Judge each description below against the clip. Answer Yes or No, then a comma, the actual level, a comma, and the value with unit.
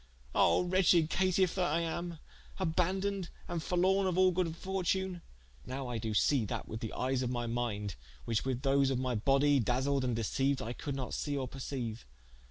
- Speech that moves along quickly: No, average, 185 wpm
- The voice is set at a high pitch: No, medium, 140 Hz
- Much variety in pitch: Yes, wide, 6.3 semitones